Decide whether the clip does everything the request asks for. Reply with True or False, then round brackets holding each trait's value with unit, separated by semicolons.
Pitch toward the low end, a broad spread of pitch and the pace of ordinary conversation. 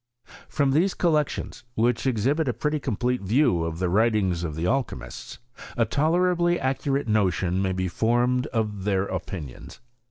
True (115 Hz; 6.9 semitones; 155 wpm)